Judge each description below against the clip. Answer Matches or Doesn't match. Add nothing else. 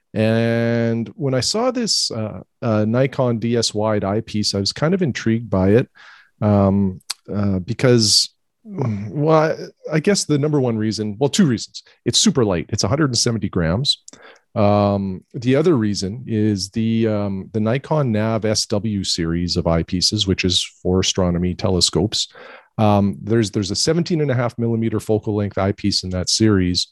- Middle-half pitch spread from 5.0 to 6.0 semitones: Doesn't match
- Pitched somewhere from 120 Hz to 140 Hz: Doesn't match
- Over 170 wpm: Doesn't match